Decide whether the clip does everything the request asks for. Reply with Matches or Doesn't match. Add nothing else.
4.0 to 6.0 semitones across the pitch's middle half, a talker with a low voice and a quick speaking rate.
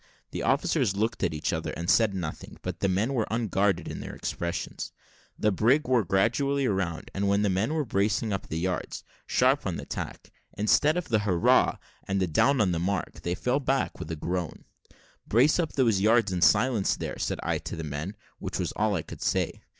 Matches